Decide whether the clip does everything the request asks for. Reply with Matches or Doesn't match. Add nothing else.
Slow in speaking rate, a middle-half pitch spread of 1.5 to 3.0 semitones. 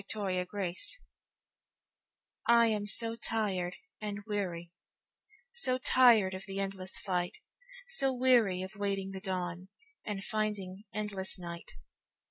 Doesn't match